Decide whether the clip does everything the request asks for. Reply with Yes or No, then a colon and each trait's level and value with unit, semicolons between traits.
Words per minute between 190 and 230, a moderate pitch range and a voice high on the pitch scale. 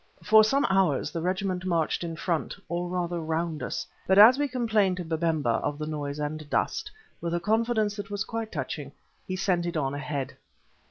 No: average, 195 wpm; average, 4.8 semitones; medium, 175 Hz